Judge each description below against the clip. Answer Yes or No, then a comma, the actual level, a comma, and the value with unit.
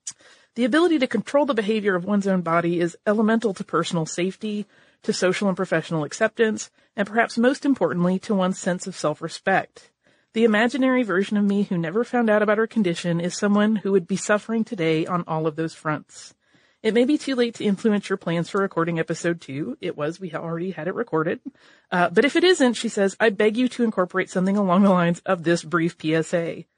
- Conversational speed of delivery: No, fast, 210 wpm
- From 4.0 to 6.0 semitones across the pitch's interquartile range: Yes, average, 4.7 semitones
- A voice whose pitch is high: Yes, high, 195 Hz